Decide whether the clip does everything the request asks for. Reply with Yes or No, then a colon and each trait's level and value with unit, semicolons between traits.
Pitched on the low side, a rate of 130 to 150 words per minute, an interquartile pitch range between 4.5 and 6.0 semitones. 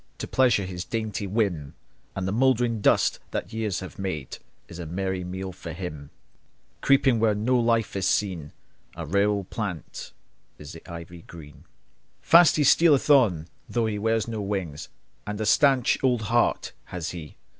No: low, 100 Hz; average, 165 wpm; average, 4.8 semitones